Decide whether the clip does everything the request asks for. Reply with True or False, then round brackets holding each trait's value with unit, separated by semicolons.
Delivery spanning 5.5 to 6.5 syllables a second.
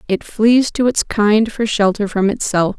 False (4.2 syllables/s)